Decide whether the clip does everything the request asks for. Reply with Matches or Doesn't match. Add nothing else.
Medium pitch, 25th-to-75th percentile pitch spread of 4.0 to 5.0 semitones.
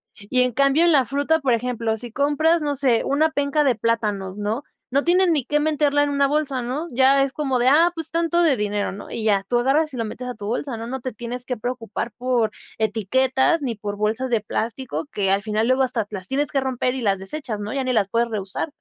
Doesn't match